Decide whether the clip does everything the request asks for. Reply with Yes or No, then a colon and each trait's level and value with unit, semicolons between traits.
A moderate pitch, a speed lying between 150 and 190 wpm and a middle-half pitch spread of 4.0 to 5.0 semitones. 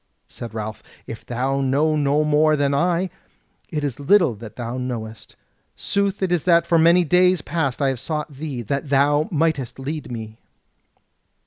Yes: medium, 145 Hz; average, 165 wpm; average, 4.5 semitones